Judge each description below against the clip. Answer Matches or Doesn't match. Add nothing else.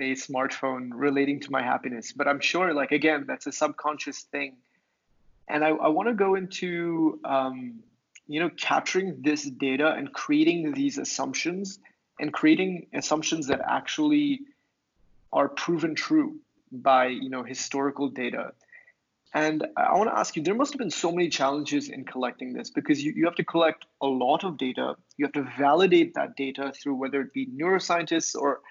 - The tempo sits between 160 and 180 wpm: Matches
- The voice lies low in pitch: Doesn't match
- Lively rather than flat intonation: Matches